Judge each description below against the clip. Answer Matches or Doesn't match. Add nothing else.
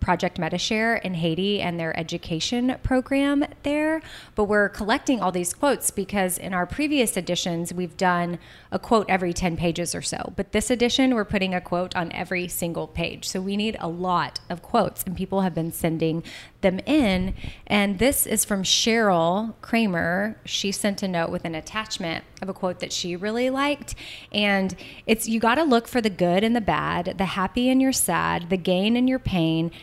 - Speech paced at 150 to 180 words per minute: Doesn't match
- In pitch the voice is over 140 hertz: Matches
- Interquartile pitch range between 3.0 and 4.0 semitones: Doesn't match